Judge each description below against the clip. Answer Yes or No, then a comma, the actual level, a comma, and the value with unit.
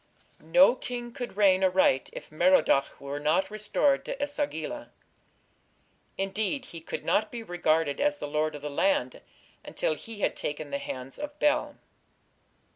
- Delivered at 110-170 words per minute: Yes, average, 155 wpm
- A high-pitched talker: Yes, high, 195 Hz